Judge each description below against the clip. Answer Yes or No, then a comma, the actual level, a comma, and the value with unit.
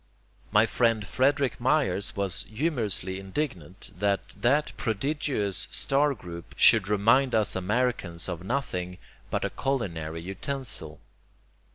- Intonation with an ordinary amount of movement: No, wide, 6.3 semitones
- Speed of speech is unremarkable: No, slow, 110 wpm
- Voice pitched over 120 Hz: No, low, 105 Hz